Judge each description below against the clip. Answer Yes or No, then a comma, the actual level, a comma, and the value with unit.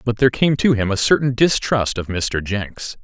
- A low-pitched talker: Yes, low, 115 Hz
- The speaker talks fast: Yes, fast, 215 wpm